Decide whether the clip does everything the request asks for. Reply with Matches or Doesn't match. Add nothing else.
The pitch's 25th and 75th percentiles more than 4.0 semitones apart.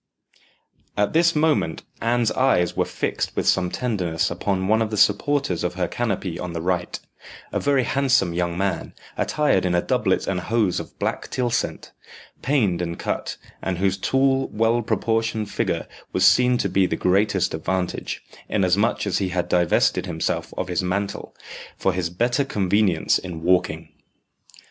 Matches